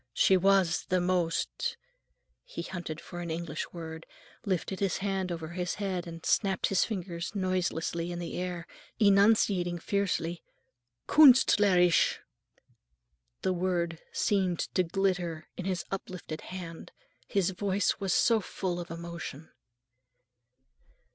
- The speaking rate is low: Yes, slow, 130 wpm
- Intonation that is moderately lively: No, narrow, 2.2 semitones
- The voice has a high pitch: No, medium, 180 Hz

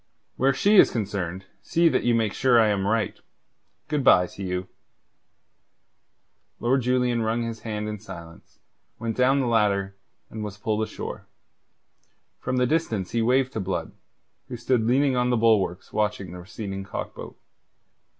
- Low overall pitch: Yes, low, 110 Hz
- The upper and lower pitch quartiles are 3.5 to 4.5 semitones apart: Yes, average, 4.0 semitones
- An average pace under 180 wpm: Yes, average, 165 wpm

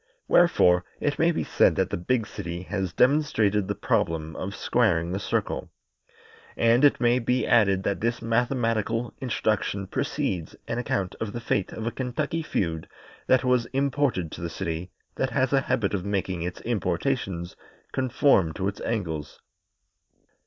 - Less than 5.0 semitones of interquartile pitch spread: No, wide, 5.6 semitones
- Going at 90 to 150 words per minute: No, average, 160 wpm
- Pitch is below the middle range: Yes, low, 110 Hz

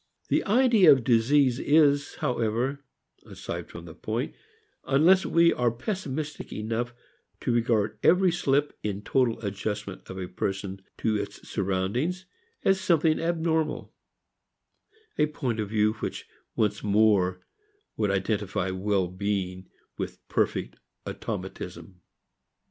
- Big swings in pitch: Yes, wide, 6.7 semitones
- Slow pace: Yes, slow, 120 wpm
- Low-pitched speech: Yes, low, 115 Hz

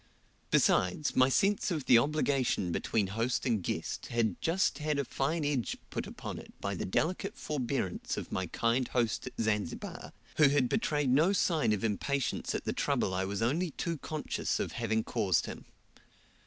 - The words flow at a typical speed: Yes, average, 175 wpm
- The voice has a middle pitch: No, low, 130 Hz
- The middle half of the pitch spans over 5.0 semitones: Yes, wide, 5.6 semitones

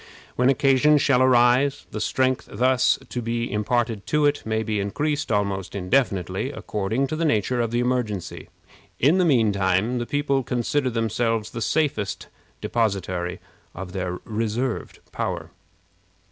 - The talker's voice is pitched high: No, low, 120 Hz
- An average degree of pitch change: Yes, average, 4.1 semitones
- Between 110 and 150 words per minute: Yes, average, 145 wpm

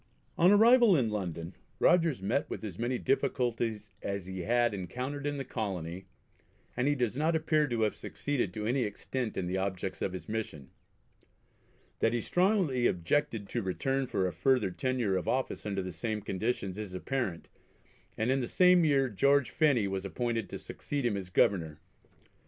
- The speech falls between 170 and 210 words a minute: Yes, average, 175 wpm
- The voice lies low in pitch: Yes, low, 115 Hz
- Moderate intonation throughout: No, wide, 5.9 semitones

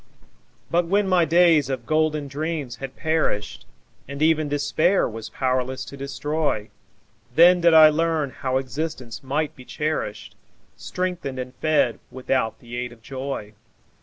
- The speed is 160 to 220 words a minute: No, average, 140 wpm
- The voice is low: No, medium, 145 Hz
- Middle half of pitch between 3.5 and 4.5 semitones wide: Yes, average, 3.8 semitones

